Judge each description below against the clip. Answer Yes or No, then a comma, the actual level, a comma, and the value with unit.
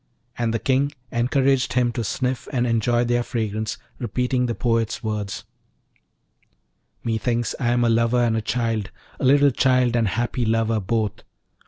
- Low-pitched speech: Yes, low, 120 Hz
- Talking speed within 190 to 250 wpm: No, average, 155 wpm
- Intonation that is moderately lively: No, narrow, 1.8 semitones